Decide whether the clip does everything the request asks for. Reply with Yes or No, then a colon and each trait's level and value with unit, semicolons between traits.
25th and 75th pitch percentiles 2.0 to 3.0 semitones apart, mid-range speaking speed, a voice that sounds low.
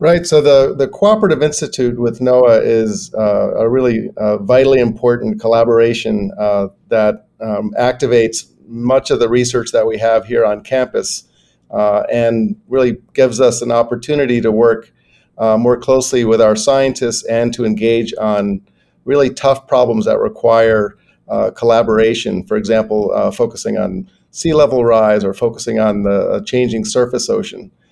Yes: average, 2.7 semitones; average, 155 wpm; low, 115 Hz